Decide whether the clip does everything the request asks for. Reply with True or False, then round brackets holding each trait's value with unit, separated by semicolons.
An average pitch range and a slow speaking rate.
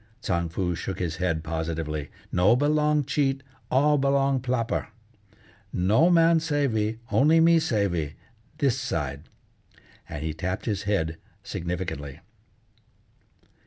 False (9.0 semitones; 115 wpm)